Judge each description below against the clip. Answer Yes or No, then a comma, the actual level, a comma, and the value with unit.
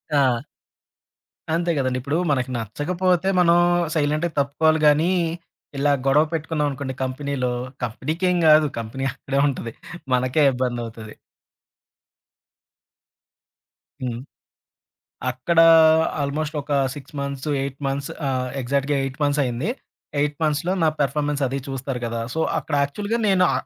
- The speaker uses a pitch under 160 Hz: Yes, medium, 140 Hz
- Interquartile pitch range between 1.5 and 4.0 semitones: Yes, average, 3.2 semitones